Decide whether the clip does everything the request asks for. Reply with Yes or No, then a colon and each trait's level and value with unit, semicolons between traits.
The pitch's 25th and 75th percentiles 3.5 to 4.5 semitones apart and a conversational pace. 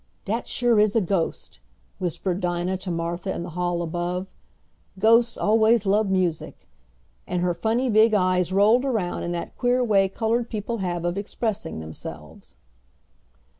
Yes: average, 4.0 semitones; average, 150 wpm